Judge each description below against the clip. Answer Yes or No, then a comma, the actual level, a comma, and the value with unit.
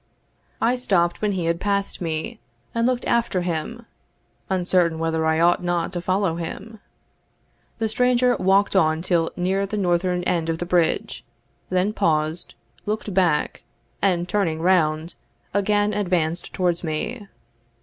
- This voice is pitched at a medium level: Yes, medium, 180 Hz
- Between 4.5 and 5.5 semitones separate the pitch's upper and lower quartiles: No, average, 3.5 semitones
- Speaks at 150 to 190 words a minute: No, average, 140 wpm